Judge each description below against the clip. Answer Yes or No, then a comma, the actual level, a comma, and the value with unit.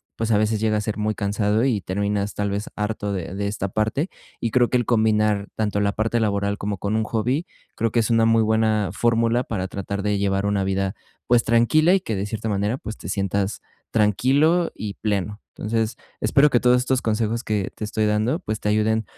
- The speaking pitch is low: Yes, low, 110 Hz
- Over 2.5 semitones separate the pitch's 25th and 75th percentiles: No, narrow, 2.0 semitones